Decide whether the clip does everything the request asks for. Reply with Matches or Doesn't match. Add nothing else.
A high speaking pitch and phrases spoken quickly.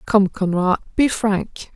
Doesn't match